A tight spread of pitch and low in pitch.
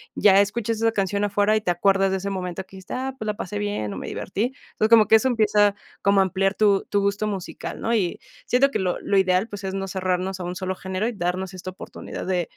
No: narrow, 2.1 semitones; high, 195 Hz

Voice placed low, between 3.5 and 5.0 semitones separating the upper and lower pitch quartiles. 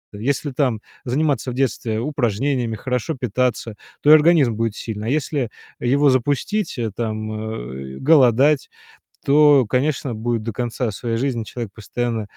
Yes: low, 125 Hz; average, 4.0 semitones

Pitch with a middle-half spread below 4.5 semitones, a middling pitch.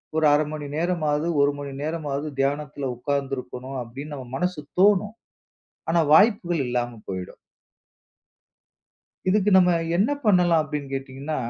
Yes: average, 4.1 semitones; medium, 150 Hz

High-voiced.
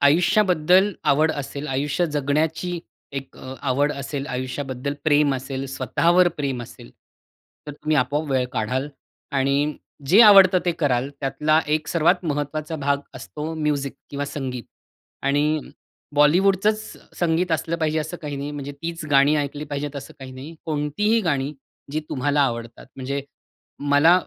No: medium, 145 Hz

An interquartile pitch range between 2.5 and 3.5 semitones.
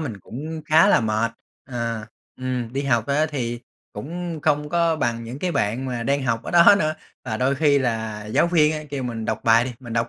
No: average, 4.7 semitones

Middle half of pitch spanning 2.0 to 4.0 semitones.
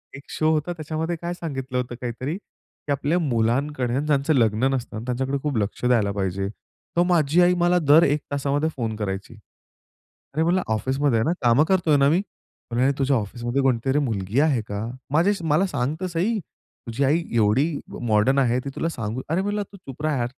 No: average, 4.9 semitones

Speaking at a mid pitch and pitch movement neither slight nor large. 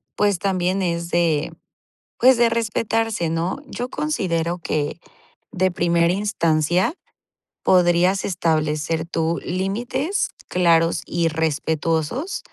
Yes: medium, 175 Hz; average, 3.5 semitones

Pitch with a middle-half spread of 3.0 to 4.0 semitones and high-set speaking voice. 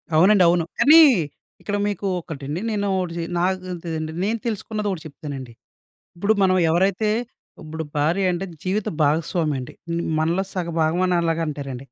No: average, 3.6 semitones; medium, 175 Hz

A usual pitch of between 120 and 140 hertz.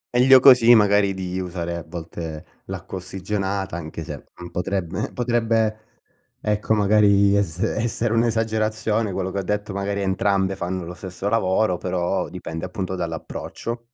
No: low, 100 Hz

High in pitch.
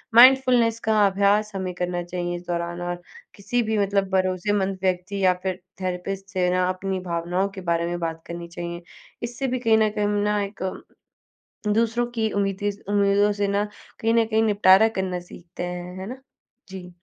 Yes: high, 195 Hz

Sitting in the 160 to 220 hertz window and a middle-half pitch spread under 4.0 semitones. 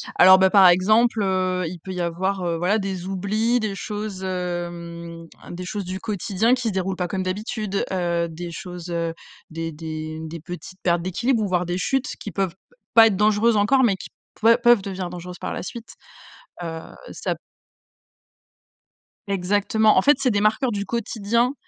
Yes: high, 190 Hz; average, 3.3 semitones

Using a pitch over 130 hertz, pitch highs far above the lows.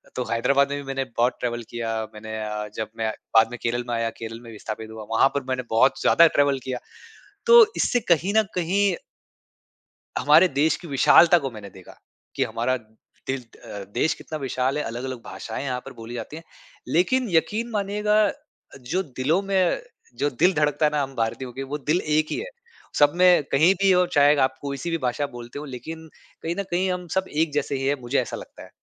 Yes: medium, 140 Hz; wide, 5.9 semitones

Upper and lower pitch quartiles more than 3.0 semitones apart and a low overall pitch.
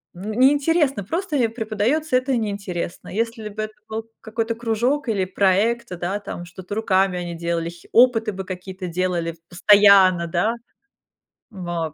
No: average, 4.2 semitones; high, 205 Hz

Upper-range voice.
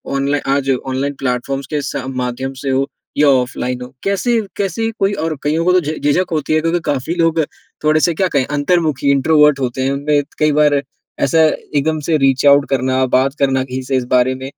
No: medium, 140 Hz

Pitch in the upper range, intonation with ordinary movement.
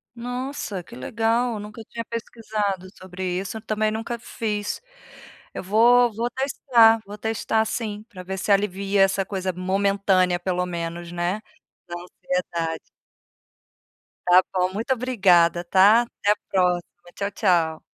Yes: high, 200 Hz; average, 3.7 semitones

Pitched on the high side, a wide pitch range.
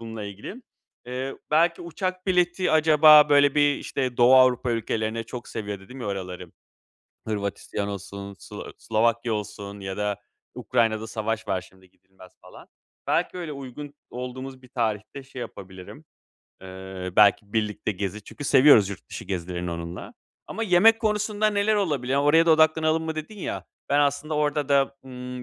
No: low, 125 Hz; wide, 6.7 semitones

